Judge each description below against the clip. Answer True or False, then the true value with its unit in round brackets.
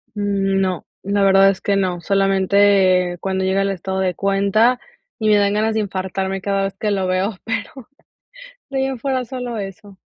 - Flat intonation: True (1.6 semitones)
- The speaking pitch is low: False (195 Hz)